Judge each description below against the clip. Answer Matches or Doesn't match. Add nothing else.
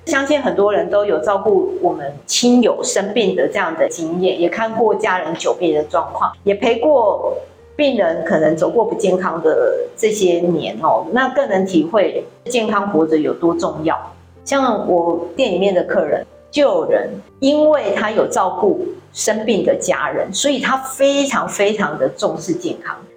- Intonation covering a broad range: Matches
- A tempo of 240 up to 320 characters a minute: Matches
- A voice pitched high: Matches